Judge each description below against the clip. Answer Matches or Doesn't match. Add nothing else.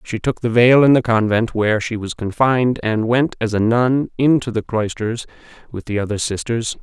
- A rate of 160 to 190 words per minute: Doesn't match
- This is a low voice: Matches